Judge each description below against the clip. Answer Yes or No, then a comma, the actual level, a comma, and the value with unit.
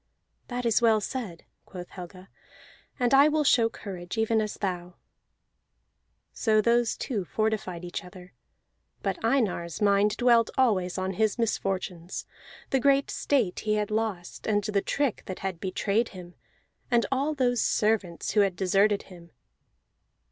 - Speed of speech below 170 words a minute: Yes, average, 145 wpm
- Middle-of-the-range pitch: No, high, 210 Hz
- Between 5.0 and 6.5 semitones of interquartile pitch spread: No, average, 4.1 semitones